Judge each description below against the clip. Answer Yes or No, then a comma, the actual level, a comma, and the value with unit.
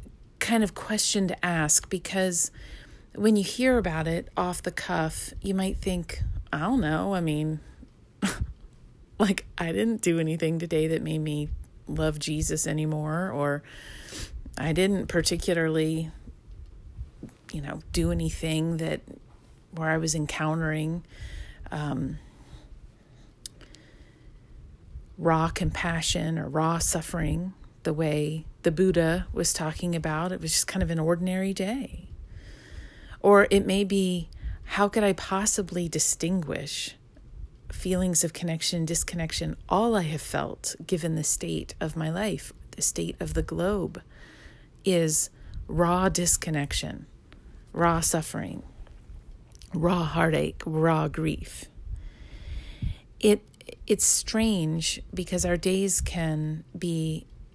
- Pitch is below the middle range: No, medium, 165 Hz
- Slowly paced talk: Yes, slow, 120 wpm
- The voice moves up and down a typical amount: Yes, average, 3.0 semitones